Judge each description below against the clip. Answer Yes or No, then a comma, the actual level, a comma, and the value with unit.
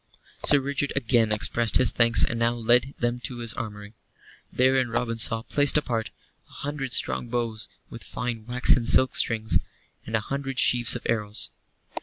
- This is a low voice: Yes, low, 120 Hz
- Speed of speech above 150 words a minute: Yes, average, 165 wpm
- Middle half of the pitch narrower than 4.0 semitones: Yes, narrow, 2.4 semitones